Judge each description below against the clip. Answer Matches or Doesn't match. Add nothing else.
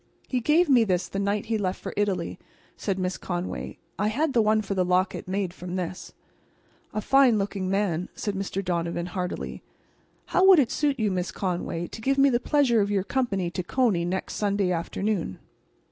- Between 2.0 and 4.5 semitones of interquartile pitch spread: Matches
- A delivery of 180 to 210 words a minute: Matches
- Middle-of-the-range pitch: Doesn't match